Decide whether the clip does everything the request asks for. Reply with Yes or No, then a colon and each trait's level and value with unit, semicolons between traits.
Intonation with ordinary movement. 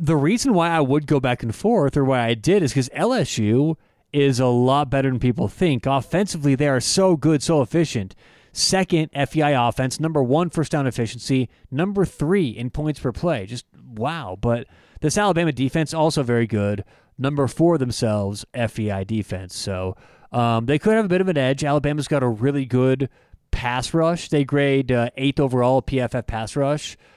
Yes: average, 4.4 semitones